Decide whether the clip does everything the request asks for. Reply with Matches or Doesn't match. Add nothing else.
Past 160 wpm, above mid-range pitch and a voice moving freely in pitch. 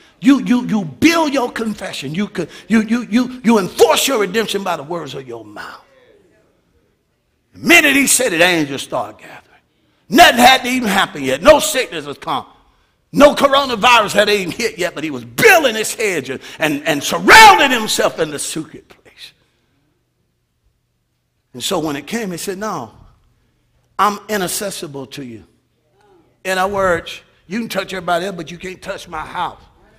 Matches